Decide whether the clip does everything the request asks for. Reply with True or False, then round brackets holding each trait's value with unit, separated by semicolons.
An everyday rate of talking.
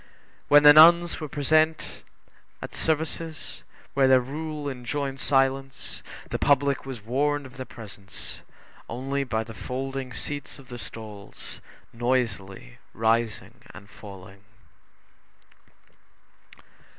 False (110 wpm)